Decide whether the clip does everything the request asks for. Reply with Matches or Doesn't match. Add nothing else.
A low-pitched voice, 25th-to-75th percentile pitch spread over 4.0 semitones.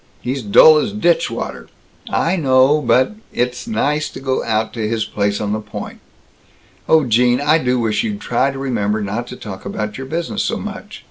Matches